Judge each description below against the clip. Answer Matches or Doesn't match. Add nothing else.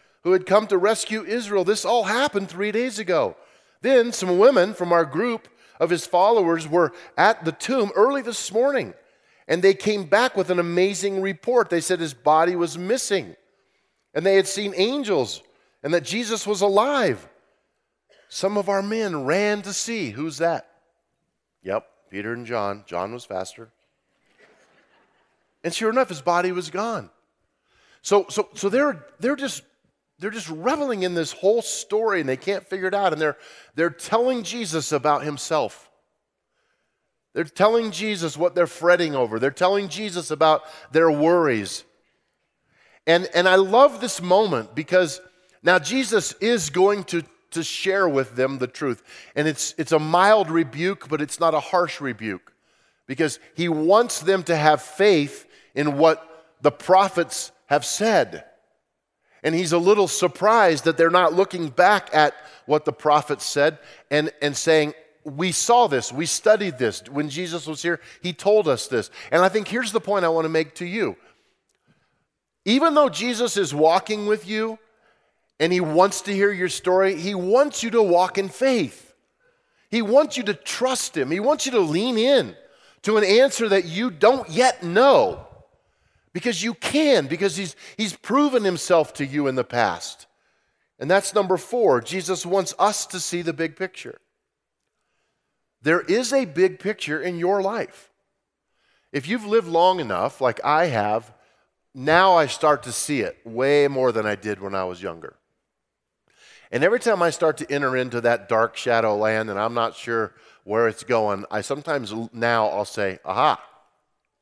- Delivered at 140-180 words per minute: Matches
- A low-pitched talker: Doesn't match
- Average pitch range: Doesn't match